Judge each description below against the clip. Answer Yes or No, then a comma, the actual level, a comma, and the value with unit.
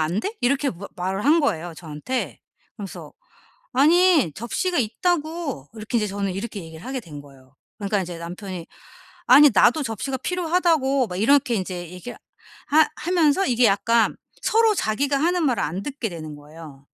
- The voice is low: No, high, 225 Hz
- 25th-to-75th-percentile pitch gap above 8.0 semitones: Yes, wide, 8.4 semitones